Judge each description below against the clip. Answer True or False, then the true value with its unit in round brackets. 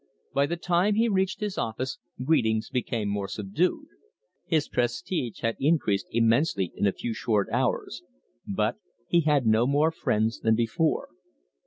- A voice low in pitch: True (125 Hz)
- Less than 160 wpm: True (150 wpm)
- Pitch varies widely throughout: True (6.8 semitones)